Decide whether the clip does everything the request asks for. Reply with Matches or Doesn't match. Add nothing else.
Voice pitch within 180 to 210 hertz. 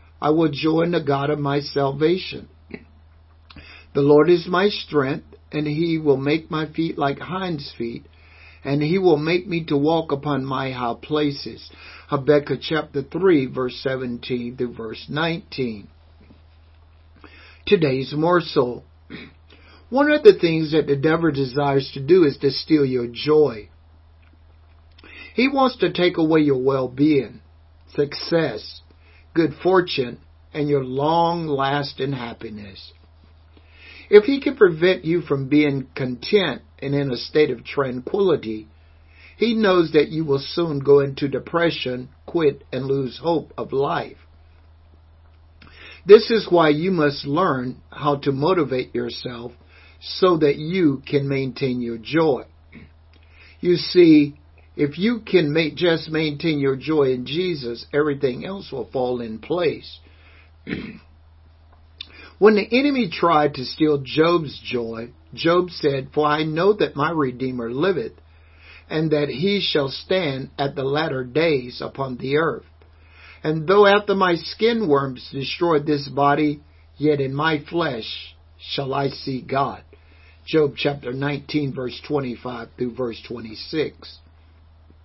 Doesn't match